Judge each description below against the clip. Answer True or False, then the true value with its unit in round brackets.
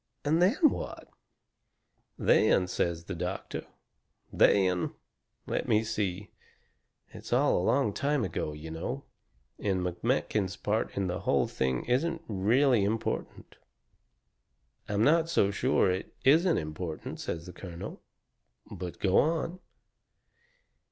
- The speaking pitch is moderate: False (100 Hz)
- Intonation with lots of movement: True (7.1 semitones)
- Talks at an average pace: False (120 wpm)